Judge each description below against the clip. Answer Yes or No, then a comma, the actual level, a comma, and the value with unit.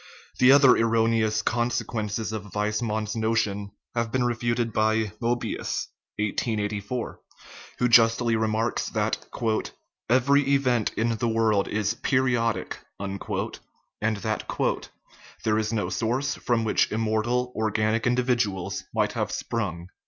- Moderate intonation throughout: No, narrow, 2.0 semitones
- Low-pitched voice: Yes, low, 115 Hz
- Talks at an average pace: No, slow, 125 wpm